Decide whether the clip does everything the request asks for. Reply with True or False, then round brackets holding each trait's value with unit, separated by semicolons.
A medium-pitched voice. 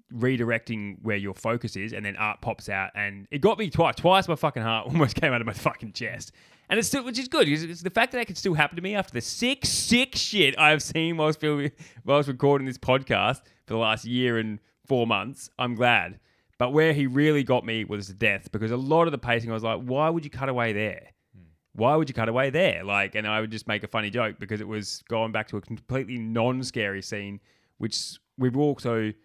False (120 Hz)